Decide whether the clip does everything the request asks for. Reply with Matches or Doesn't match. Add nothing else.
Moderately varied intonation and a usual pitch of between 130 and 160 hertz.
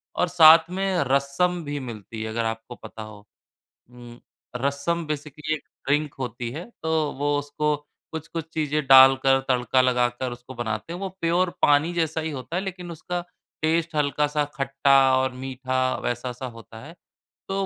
Matches